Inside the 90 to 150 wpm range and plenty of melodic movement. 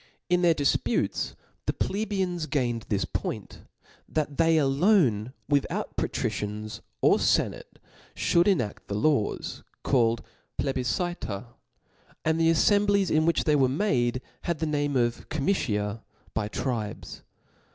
Yes: average, 140 wpm; wide, 6.0 semitones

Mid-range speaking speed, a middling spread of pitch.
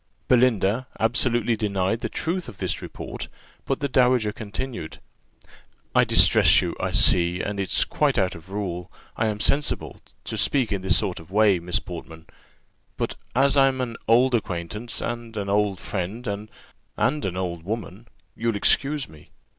Yes: average, 160 wpm; average, 4.6 semitones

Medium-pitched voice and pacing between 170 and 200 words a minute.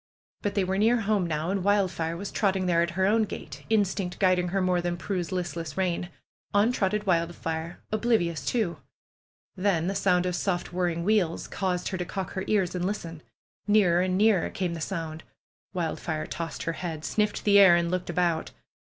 Yes: medium, 180 Hz; average, 185 wpm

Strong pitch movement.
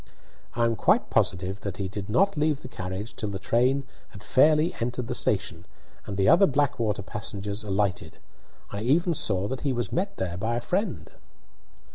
Yes: wide, 6.0 semitones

